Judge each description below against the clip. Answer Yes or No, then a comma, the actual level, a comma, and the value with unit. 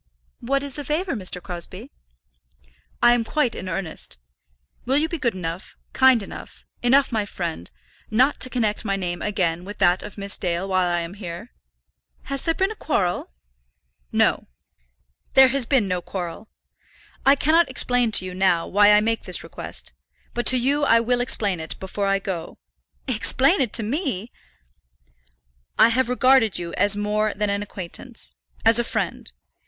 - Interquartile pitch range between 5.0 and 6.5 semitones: Yes, wide, 5.6 semitones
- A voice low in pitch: No, high, 215 Hz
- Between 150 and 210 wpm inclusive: Yes, average, 170 wpm